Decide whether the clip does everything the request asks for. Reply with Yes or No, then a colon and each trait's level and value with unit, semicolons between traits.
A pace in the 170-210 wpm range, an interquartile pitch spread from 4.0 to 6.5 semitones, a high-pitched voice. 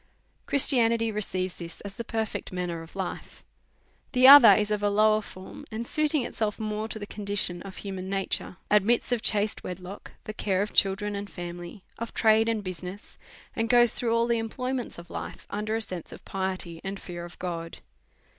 No: average, 195 wpm; average, 3.4 semitones; high, 205 Hz